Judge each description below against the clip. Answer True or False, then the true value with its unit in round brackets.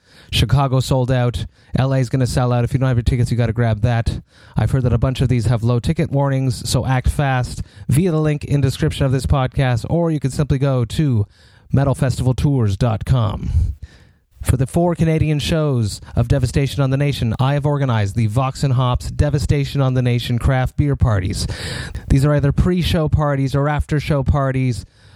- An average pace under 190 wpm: False (200 wpm)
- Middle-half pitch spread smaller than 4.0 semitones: True (3.1 semitones)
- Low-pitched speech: True (130 Hz)